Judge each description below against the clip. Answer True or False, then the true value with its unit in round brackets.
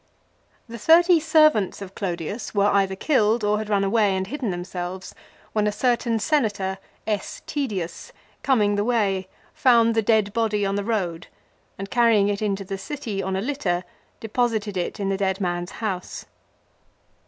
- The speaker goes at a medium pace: True (165 wpm)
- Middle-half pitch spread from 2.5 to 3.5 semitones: True (3.1 semitones)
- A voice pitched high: True (205 Hz)